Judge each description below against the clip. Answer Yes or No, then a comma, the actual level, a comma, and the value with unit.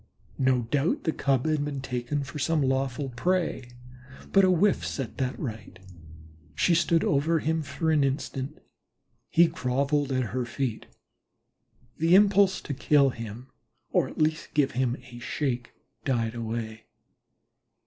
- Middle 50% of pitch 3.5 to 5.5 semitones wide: Yes, average, 4.1 semitones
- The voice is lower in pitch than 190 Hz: Yes, medium, 140 Hz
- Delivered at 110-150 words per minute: Yes, average, 145 wpm